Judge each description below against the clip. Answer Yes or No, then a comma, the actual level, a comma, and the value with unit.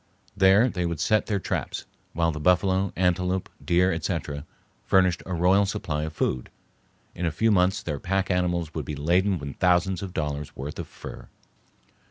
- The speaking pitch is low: Yes, very low, 90 Hz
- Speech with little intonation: No, average, 3.2 semitones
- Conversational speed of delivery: Yes, average, 175 wpm